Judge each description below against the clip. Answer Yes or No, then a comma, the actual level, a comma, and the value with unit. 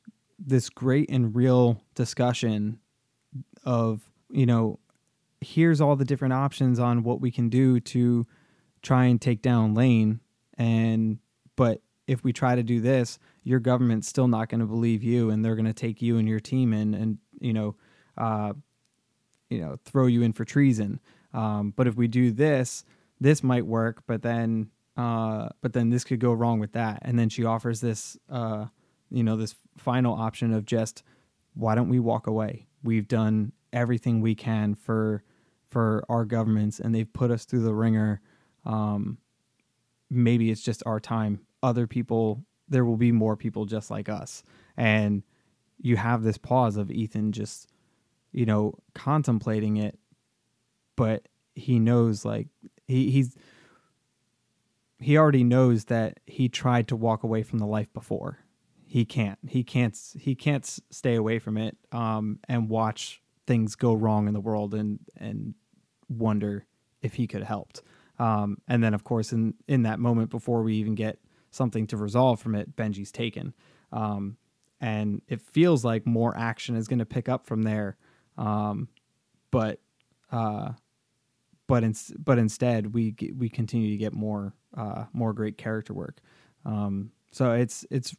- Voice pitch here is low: Yes, low, 115 Hz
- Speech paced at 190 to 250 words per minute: No, average, 165 wpm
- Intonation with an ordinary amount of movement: No, narrow, 2.3 semitones